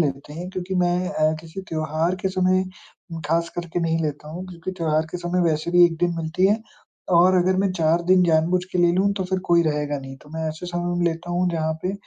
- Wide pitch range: No, narrow, 2.4 semitones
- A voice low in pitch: No, medium, 175 Hz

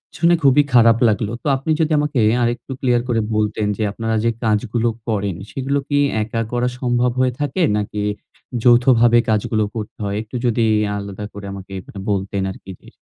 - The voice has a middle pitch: No, low, 115 Hz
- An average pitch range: Yes, average, 3.2 semitones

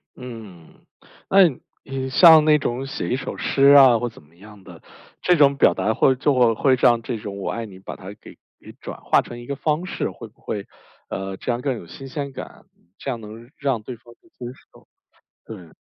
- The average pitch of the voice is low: Yes, low, 120 Hz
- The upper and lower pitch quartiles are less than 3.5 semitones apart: No, average, 4.1 semitones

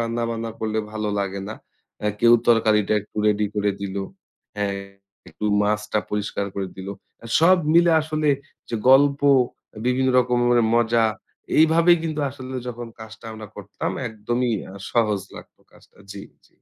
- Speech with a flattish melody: No, average, 3.4 semitones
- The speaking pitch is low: Yes, low, 115 Hz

